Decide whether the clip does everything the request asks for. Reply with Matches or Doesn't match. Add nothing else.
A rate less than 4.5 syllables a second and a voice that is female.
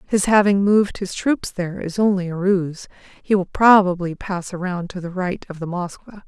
Doesn't match